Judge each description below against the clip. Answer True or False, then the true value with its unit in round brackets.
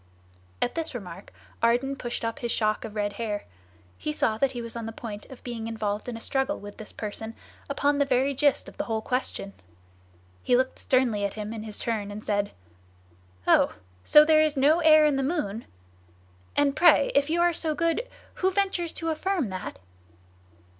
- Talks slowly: False (195 wpm)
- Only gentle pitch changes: False (5.4 semitones)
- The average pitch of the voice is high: True (245 Hz)